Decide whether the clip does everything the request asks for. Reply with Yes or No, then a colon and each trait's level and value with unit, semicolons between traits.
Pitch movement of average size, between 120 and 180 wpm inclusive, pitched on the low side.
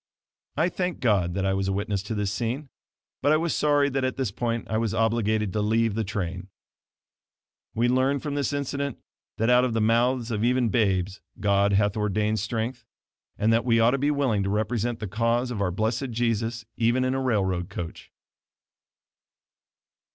No: average, 3.6 semitones; average, 190 wpm; low, 115 Hz